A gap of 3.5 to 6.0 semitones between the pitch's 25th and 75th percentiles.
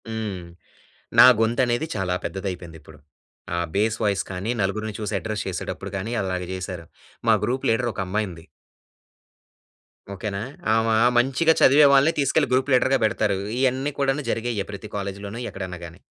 Yes: average, 4.2 semitones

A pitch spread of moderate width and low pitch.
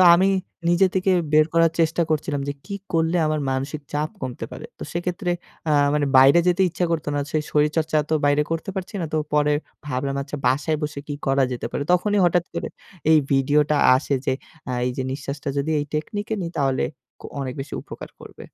No: average, 3.2 semitones; medium, 150 Hz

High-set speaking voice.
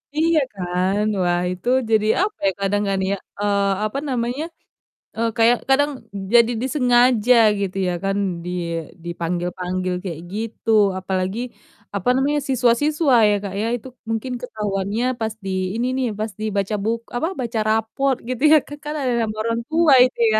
Yes: high, 225 Hz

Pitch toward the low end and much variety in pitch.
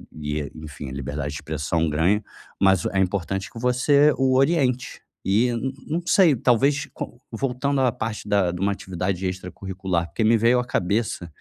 Yes: low, 100 Hz; wide, 6.2 semitones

